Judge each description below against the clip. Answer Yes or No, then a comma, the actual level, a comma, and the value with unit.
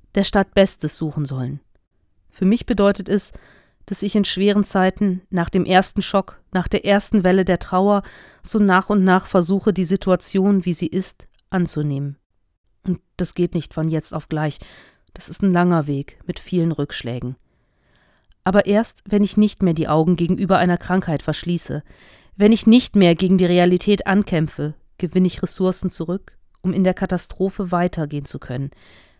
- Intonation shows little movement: No, average, 3.9 semitones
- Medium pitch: Yes, medium, 180 Hz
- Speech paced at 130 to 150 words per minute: No, average, 170 wpm